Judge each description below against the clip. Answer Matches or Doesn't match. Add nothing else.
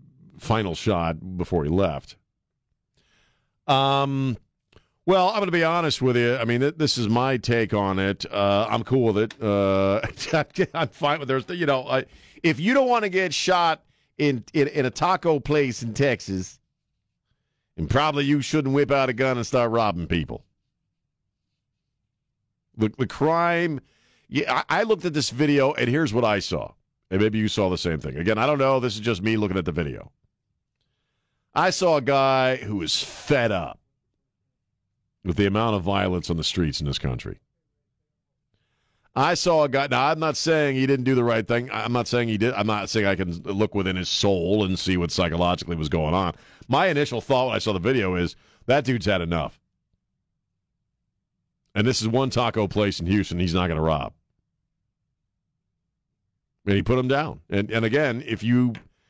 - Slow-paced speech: Doesn't match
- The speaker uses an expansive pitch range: Matches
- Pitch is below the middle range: Matches